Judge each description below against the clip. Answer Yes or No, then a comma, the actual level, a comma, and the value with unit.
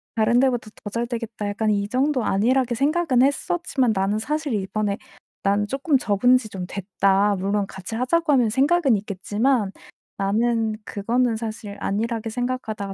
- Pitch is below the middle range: No, high, 225 Hz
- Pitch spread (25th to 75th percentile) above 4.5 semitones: No, average, 3.8 semitones